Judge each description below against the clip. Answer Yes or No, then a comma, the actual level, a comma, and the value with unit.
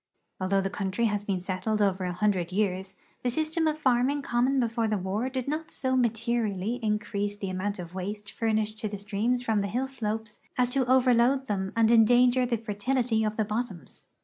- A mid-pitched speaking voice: No, high, 220 Hz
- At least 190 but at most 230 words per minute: Yes, average, 195 wpm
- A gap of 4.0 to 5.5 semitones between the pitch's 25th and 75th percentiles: No, average, 3.6 semitones